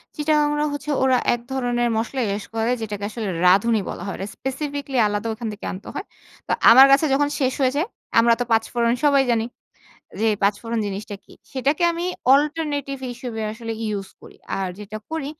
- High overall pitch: Yes, high, 240 Hz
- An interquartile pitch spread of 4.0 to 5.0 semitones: Yes, average, 4.3 semitones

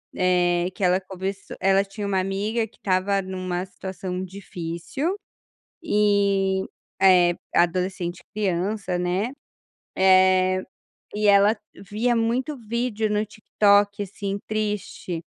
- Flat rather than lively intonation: Yes, narrow, 2.2 semitones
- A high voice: Yes, high, 195 Hz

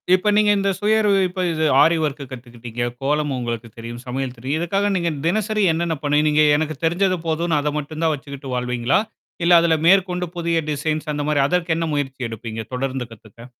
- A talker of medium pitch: Yes, medium, 150 Hz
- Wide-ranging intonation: No, average, 4.9 semitones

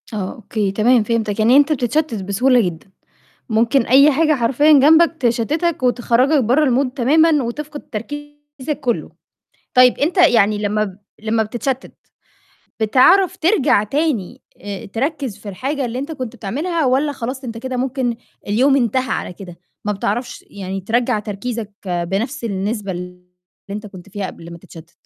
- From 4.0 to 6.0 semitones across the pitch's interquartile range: Yes, average, 5.1 semitones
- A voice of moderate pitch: No, high, 240 Hz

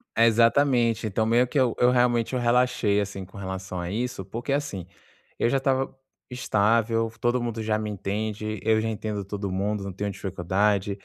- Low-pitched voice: Yes, low, 110 Hz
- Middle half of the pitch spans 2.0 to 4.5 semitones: Yes, average, 3.2 semitones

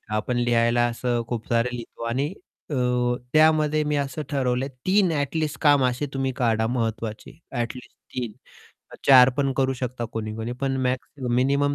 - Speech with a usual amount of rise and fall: Yes, average, 3.2 semitones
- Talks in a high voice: No, low, 130 Hz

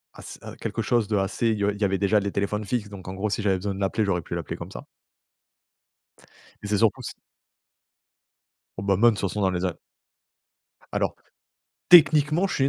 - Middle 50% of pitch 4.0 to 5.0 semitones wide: No, narrow, 2.4 semitones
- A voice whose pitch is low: Yes, low, 100 Hz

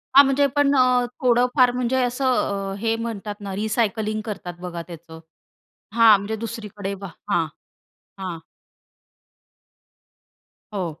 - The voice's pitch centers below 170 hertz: No, high, 220 Hz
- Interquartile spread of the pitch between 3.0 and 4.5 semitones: Yes, average, 4.2 semitones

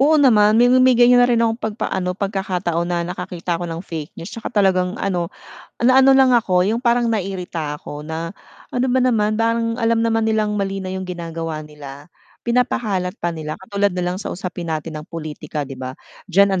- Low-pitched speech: No, high, 190 Hz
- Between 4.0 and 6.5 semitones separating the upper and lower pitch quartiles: Yes, wide, 5.4 semitones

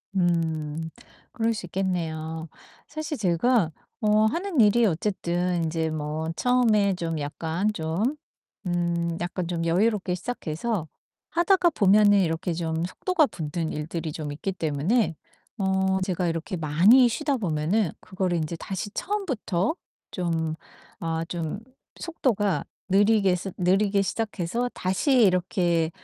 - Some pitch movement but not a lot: Yes, average, 4.5 semitones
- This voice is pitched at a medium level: Yes, medium, 180 Hz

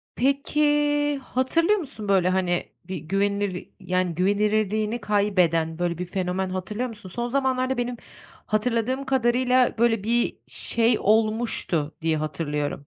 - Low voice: No, high, 210 Hz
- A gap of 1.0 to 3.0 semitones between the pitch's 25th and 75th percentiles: No, average, 4.9 semitones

